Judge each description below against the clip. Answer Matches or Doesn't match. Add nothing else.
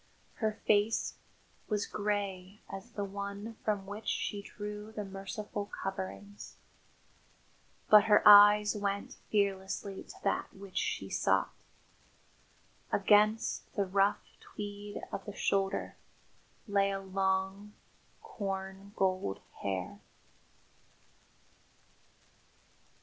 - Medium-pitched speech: Doesn't match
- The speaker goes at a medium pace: Doesn't match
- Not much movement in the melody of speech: Matches